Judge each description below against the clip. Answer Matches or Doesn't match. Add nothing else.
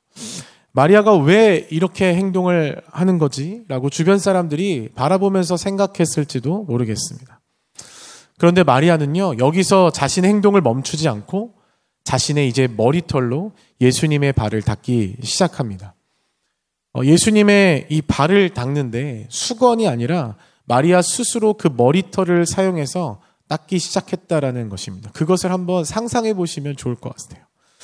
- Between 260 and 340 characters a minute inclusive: Matches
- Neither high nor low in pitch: Matches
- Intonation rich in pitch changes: Matches